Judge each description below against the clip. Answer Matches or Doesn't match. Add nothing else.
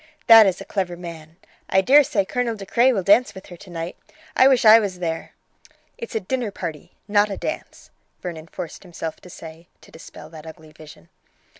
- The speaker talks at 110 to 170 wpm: Doesn't match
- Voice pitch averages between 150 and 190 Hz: Matches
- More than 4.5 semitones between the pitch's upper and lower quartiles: Matches